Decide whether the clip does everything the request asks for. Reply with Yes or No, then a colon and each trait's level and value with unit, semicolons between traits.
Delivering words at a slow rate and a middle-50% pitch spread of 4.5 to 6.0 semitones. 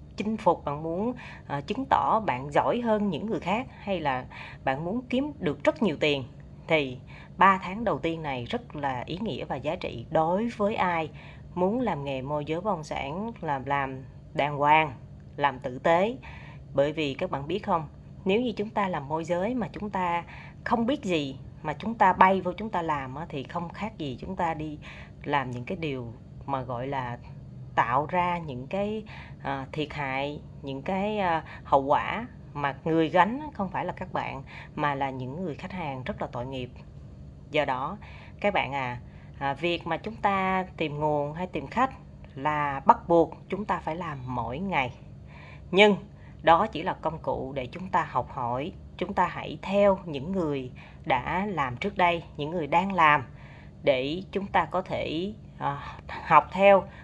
No: average, 185 wpm; average, 5.3 semitones